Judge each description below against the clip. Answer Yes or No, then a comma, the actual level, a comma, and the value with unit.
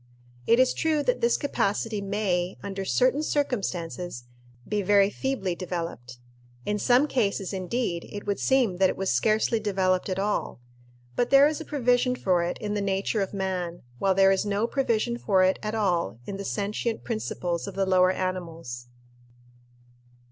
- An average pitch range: Yes, average, 4.0 semitones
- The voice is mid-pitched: No, high, 200 Hz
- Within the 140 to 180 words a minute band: Yes, average, 170 wpm